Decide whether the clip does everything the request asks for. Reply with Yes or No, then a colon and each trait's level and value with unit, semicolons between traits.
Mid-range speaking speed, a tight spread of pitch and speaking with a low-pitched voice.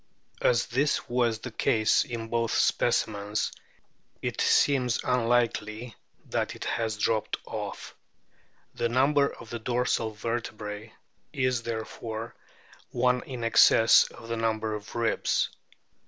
No: slow, 120 wpm; narrow, 1.7 semitones; low, 115 Hz